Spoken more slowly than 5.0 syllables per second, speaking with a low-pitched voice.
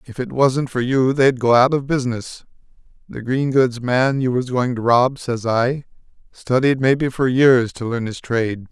Yes: 4.5 syllables/s; low, 125 Hz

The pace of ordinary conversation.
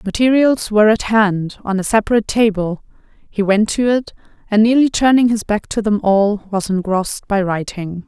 Yes: average, 180 wpm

